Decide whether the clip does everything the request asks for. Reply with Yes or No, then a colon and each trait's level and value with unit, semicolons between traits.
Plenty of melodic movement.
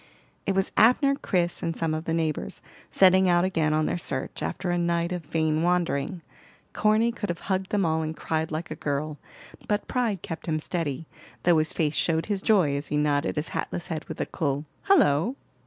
No: average, 3.3 semitones